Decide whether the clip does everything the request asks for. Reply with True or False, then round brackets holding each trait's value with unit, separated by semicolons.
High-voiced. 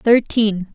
True (215 Hz)